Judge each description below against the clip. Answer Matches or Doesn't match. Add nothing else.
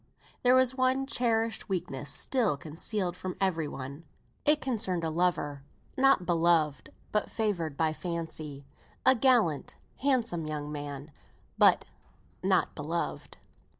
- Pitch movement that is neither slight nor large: Doesn't match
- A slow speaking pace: Matches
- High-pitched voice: Doesn't match